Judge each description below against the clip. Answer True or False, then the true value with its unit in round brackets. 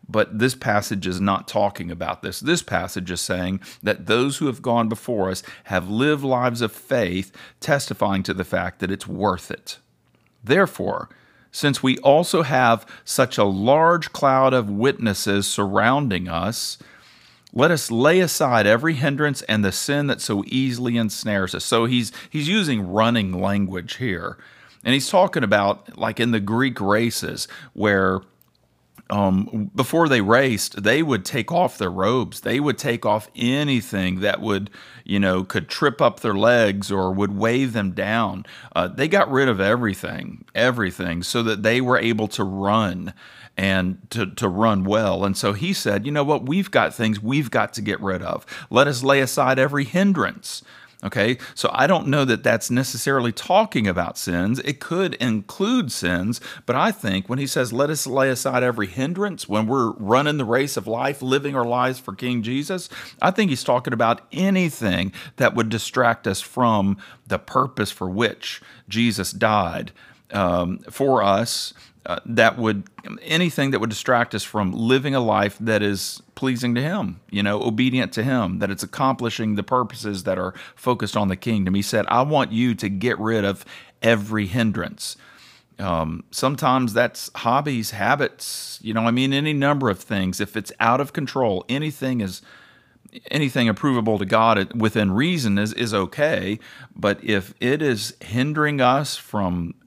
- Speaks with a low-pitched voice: True (115 Hz)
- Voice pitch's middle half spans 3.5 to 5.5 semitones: True (4.8 semitones)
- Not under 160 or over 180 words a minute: True (170 wpm)